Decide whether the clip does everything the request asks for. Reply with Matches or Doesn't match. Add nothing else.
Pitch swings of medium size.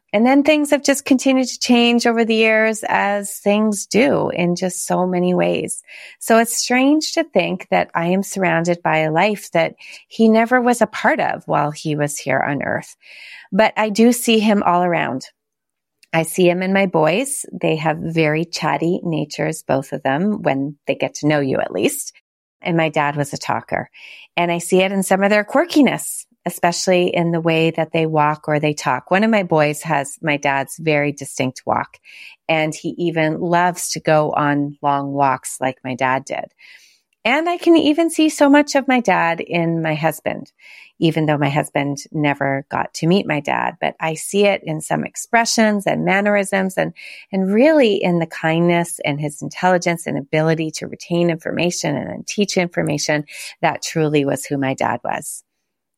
Doesn't match